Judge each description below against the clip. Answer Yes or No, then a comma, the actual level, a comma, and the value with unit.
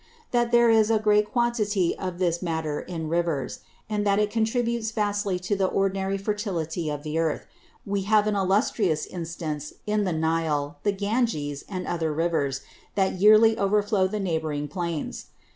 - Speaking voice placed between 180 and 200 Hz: Yes, high, 190 Hz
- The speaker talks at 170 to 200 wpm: No, average, 160 wpm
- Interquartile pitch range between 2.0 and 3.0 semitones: No, average, 4.5 semitones